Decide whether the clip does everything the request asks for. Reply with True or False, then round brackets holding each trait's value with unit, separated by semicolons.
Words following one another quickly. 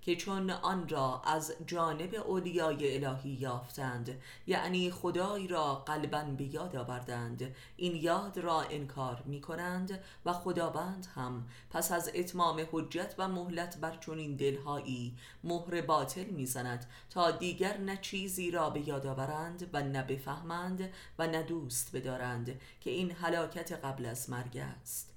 False (145 wpm)